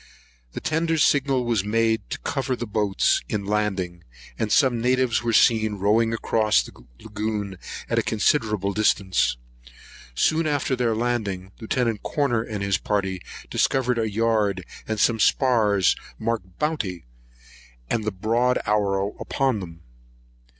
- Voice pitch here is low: Yes, low, 110 Hz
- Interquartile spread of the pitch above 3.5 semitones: No, average, 3.2 semitones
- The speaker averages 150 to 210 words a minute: No, slow, 135 wpm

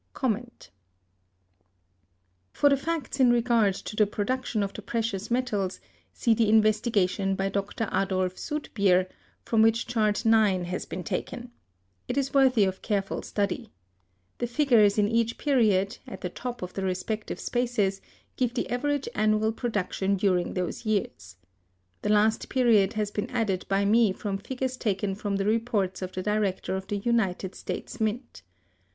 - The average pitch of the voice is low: No, high, 215 Hz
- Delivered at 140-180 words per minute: Yes, average, 155 wpm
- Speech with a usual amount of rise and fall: Yes, average, 3.4 semitones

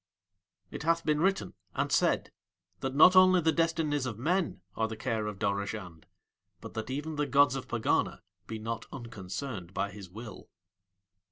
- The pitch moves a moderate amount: No, wide, 6.5 semitones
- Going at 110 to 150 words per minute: No, average, 165 wpm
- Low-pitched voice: Yes, low, 125 Hz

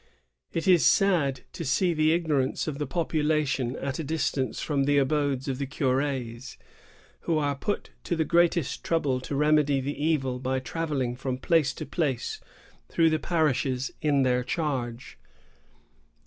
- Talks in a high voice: No, medium, 145 Hz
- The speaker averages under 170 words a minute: Yes, average, 160 wpm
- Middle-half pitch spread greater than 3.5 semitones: No, average, 3.2 semitones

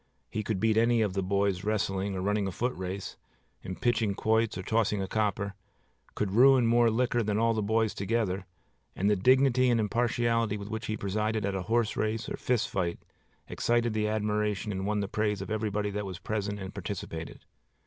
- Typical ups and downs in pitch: No, narrow, 2.3 semitones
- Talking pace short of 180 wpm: No, average, 195 wpm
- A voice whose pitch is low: Yes, low, 105 Hz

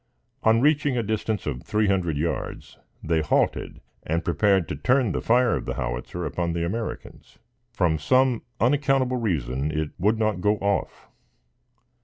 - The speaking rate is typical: Yes, average, 155 wpm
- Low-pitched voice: Yes, low, 100 Hz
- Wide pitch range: Yes, wide, 6.1 semitones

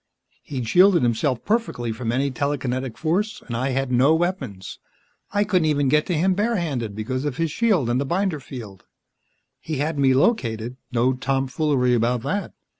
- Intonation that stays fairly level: No, average, 5.1 semitones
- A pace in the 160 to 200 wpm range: Yes, average, 170 wpm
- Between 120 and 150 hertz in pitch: Yes, low, 135 Hz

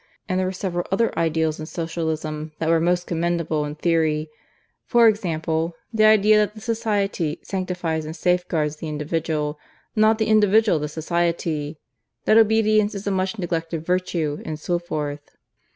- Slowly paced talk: No, average, 155 wpm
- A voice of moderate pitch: Yes, medium, 170 Hz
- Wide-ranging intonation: No, average, 4.0 semitones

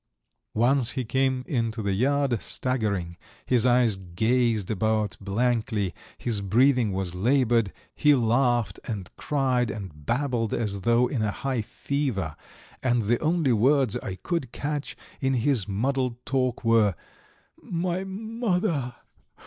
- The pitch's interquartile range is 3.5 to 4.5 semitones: Yes, average, 4.0 semitones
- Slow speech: Yes, slow, 130 wpm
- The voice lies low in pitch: Yes, low, 120 Hz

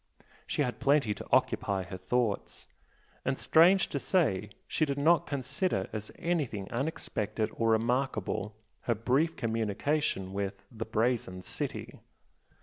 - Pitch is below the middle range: Yes, low, 115 Hz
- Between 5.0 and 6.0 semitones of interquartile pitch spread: Yes, average, 5.3 semitones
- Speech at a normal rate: No, slow, 130 wpm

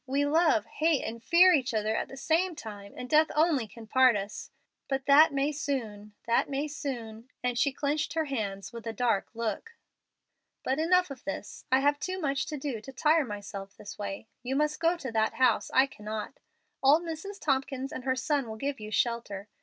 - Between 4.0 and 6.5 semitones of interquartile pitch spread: Yes, average, 5.3 semitones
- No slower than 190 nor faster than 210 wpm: Yes, average, 200 wpm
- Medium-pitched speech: No, very high, 265 Hz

